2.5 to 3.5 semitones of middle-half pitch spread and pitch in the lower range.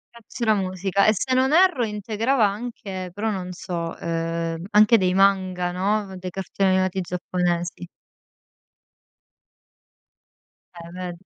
No: average, 2.9 semitones; high, 190 Hz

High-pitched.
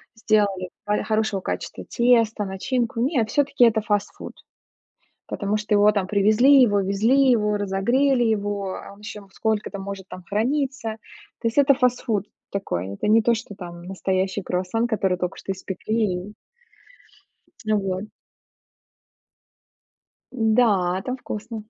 Yes: high, 210 Hz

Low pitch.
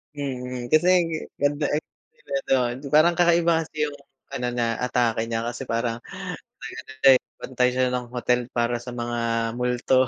Yes: low, 125 Hz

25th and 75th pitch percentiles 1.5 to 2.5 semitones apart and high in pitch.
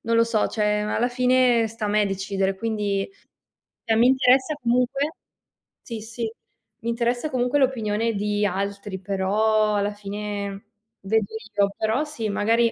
No: average, 2.9 semitones; high, 220 Hz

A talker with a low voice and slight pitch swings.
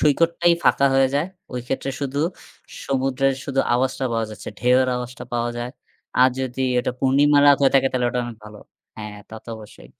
Yes: low, 130 Hz; narrow, 2.2 semitones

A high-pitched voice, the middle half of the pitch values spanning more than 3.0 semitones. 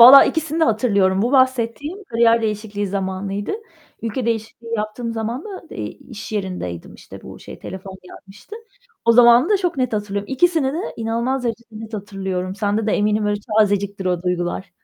Yes: high, 220 Hz; average, 3.6 semitones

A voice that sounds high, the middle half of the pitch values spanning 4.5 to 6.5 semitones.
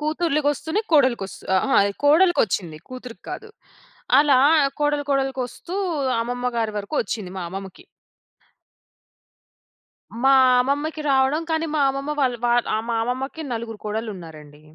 Yes: very high, 260 Hz; average, 5.0 semitones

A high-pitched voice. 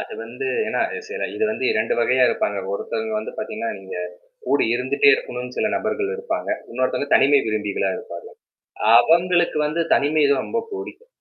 No: medium, 150 Hz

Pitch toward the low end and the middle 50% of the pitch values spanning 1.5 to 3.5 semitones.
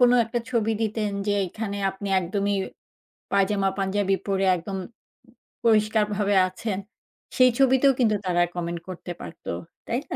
No: high, 205 Hz; narrow, 2.5 semitones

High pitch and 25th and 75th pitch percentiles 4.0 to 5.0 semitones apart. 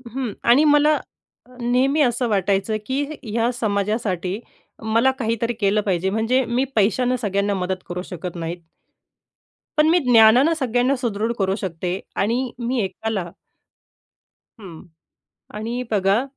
Yes: high, 220 Hz; average, 4.3 semitones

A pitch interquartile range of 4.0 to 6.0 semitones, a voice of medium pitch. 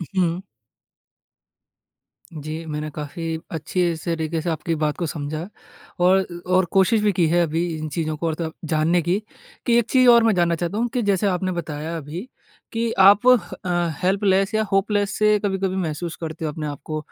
No: average, 3.6 semitones; medium, 175 Hz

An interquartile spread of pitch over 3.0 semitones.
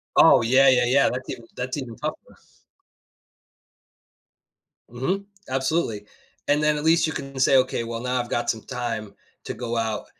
No: average, 2.7 semitones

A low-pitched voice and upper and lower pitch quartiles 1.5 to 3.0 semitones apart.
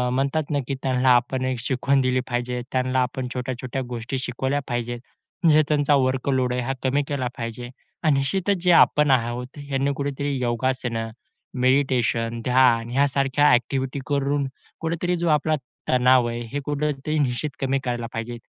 Yes: low, 130 Hz; narrow, 2.4 semitones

